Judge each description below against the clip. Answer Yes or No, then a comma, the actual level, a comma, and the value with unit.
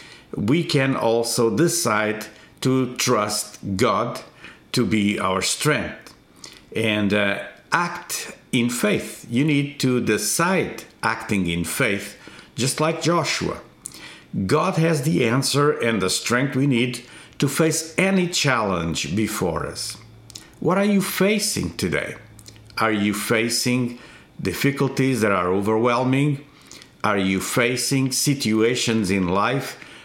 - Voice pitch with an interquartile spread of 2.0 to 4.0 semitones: No, average, 4.8 semitones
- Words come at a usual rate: No, slow, 120 wpm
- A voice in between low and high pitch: No, low, 120 Hz